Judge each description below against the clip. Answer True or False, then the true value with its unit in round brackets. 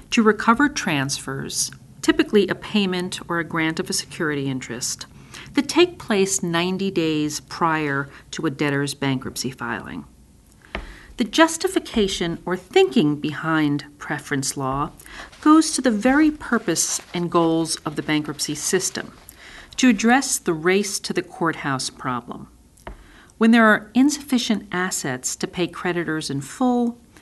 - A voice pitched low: False (175 Hz)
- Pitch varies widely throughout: True (7.2 semitones)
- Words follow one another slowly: True (130 wpm)